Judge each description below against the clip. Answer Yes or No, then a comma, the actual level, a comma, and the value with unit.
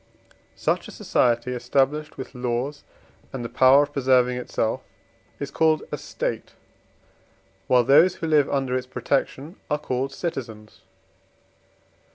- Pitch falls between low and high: No, low, 130 Hz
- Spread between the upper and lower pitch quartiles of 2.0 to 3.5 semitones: Yes, average, 2.8 semitones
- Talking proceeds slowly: Yes, slow, 130 wpm